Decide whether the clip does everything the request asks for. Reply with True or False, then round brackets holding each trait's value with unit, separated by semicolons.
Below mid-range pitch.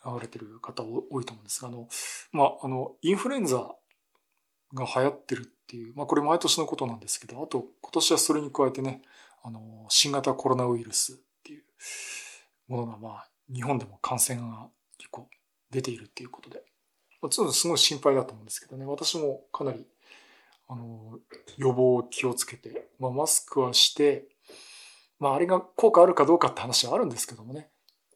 True (130 Hz)